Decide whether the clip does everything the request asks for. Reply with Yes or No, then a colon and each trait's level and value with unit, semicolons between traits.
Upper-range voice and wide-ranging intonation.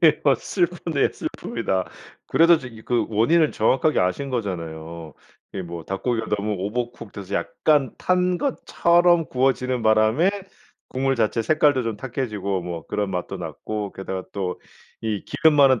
No: low, 115 Hz; wide, 6.5 semitones